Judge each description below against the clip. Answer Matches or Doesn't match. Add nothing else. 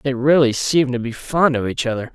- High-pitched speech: Doesn't match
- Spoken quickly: Matches